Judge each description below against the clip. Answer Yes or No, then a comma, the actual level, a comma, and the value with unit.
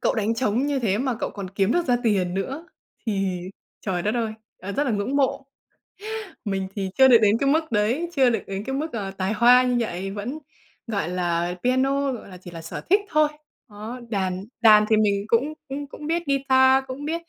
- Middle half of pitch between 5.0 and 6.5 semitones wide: Yes, wide, 5.4 semitones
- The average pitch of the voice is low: No, high, 230 Hz